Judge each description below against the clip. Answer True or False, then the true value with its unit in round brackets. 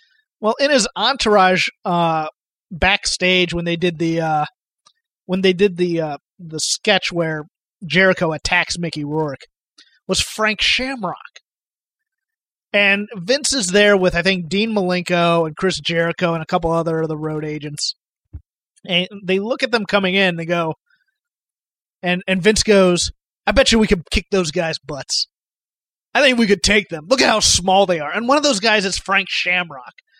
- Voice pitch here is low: False (185 Hz)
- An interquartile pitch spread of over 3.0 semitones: True (4.2 semitones)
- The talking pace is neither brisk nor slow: True (175 wpm)